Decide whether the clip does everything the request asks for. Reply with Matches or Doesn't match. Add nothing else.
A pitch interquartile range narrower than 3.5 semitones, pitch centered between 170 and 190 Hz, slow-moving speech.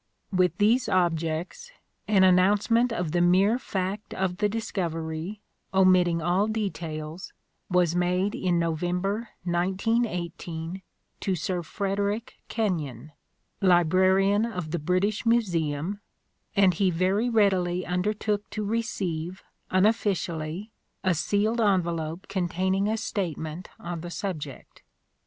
Matches